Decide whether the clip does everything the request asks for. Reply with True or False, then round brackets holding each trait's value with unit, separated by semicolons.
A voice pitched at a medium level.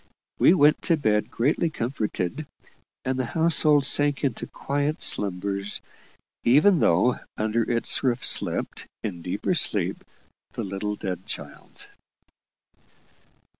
False (125 Hz)